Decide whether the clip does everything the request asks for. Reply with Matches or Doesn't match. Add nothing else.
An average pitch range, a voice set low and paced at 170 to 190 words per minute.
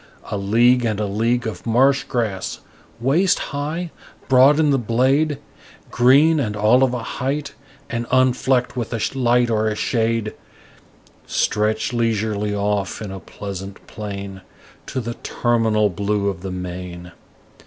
Doesn't match